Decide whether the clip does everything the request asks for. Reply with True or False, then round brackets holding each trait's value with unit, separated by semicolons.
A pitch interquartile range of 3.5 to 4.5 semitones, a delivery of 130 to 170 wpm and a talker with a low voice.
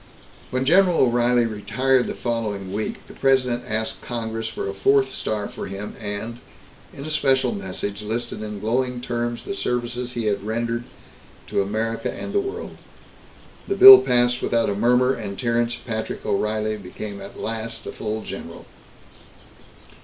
False (2.7 semitones; 155 wpm; 115 Hz)